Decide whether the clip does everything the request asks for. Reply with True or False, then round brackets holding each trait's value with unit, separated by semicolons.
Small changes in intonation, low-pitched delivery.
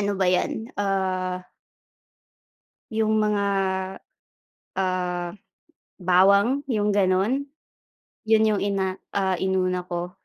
False (2.3 semitones; 195 Hz)